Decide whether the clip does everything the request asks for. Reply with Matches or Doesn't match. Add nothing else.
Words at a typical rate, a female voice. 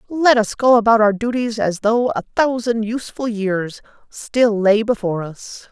Matches